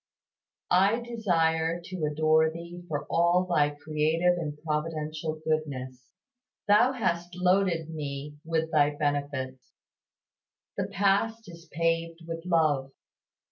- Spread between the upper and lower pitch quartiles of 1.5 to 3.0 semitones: Yes, average, 2.7 semitones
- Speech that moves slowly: Yes, slow, 110 wpm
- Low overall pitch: No, medium, 160 Hz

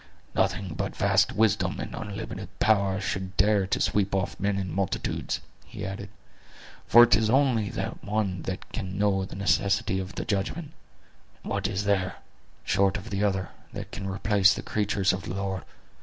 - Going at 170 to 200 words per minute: Yes, average, 175 wpm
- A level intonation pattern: Yes, narrow, 1.4 semitones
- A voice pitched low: Yes, low, 100 Hz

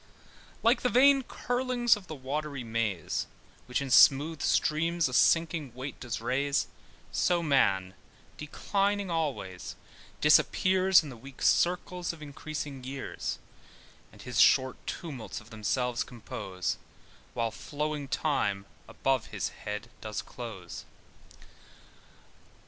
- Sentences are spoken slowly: Yes, slow, 120 wpm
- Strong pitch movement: Yes, wide, 6.1 semitones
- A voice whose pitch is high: No, medium, 140 Hz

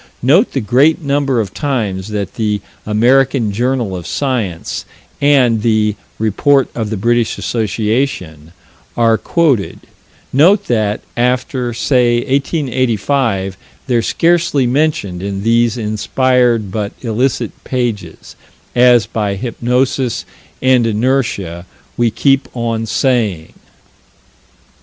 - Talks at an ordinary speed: No, slow, 105 wpm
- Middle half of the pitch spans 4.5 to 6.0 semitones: No, average, 3.8 semitones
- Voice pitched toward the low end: Yes, low, 120 Hz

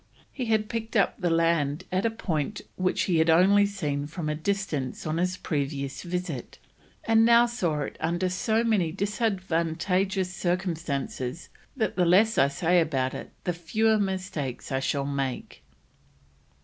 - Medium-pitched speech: Yes, medium, 180 Hz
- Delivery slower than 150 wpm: No, average, 155 wpm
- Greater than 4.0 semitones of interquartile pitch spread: Yes, average, 4.7 semitones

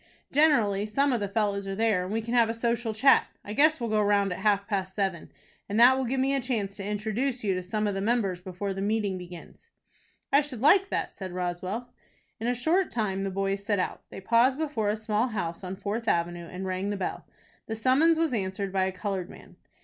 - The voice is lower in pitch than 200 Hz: No, high, 210 Hz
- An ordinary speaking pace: No, fast, 235 wpm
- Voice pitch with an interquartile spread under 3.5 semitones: No, average, 3.8 semitones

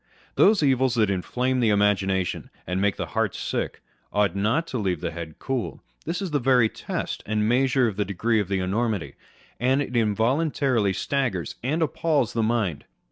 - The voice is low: Yes, low, 115 Hz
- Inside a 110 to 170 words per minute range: No, average, 180 wpm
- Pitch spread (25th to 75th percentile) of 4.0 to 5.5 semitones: Yes, average, 5.0 semitones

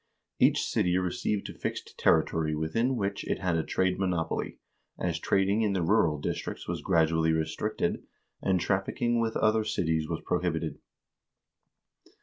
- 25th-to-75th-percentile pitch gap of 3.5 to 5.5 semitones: Yes, average, 4.2 semitones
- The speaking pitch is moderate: No, very low, 90 Hz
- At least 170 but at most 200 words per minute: No, average, 140 wpm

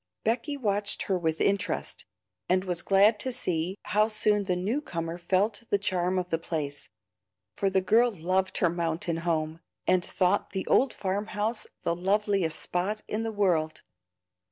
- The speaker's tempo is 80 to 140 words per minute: No, average, 165 wpm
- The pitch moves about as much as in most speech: Yes, average, 3.3 semitones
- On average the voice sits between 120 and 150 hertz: No, high, 190 Hz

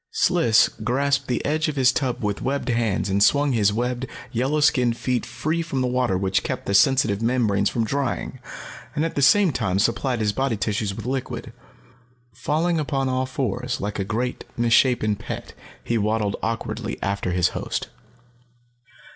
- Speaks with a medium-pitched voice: No, low, 120 Hz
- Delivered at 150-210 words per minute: Yes, average, 170 wpm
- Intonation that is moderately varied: Yes, average, 4.2 semitones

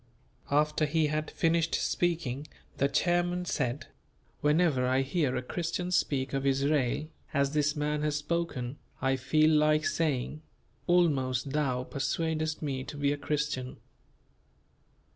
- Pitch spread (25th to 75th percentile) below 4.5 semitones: Yes, average, 2.8 semitones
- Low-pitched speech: No, medium, 150 Hz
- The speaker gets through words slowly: Yes, slow, 130 wpm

